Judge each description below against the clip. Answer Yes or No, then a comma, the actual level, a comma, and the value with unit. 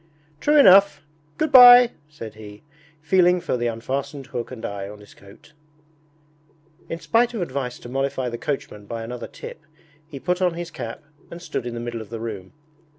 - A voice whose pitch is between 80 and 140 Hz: Yes, low, 135 Hz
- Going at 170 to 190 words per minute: Yes, average, 185 wpm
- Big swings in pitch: Yes, wide, 7.2 semitones